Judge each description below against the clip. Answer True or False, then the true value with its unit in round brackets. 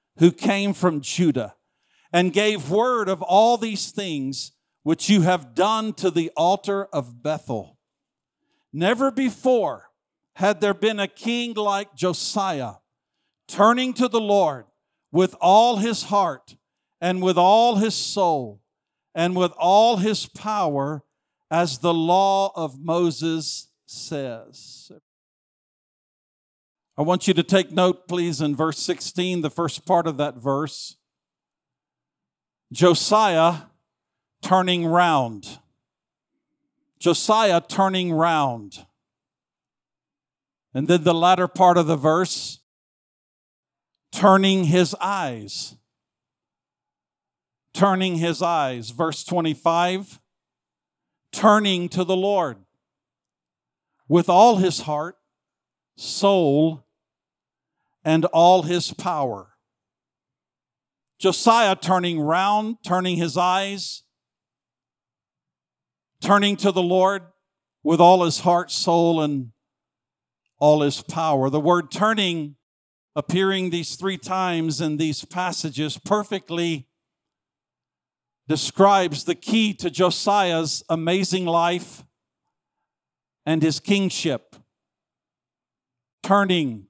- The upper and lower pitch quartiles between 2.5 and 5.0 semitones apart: True (4.1 semitones)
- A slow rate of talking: True (100 wpm)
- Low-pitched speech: False (175 Hz)